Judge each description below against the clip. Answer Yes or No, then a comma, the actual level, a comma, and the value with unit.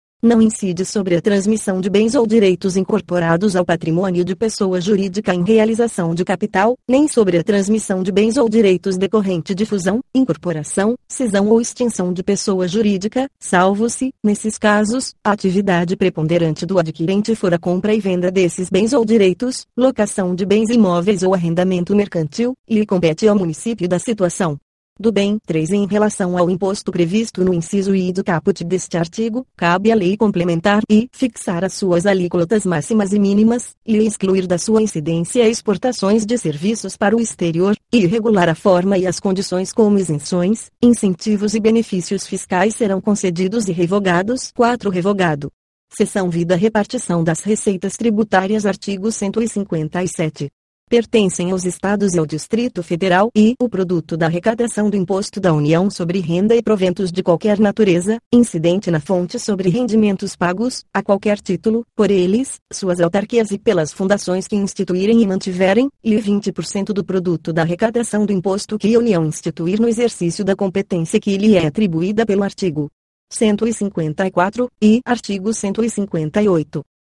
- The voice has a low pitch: No, high, 200 Hz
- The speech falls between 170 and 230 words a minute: No, average, 155 wpm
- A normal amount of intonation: Yes, average, 3.3 semitones